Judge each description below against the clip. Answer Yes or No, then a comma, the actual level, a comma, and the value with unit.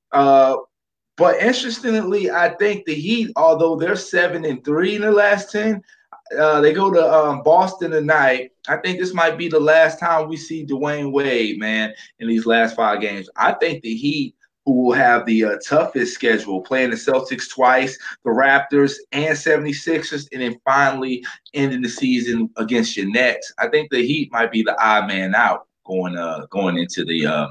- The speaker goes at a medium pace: Yes, average, 185 wpm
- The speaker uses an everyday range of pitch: No, wide, 6.2 semitones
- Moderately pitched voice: Yes, medium, 145 Hz